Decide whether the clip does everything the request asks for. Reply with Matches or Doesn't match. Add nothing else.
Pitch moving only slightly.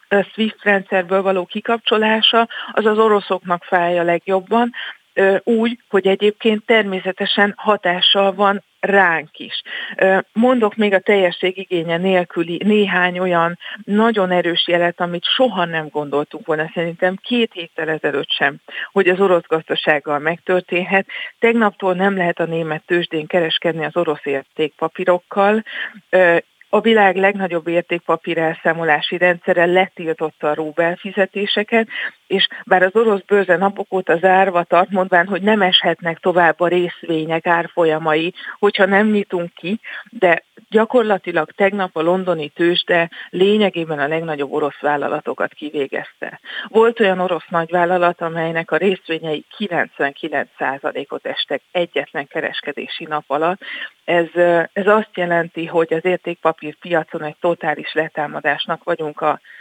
Doesn't match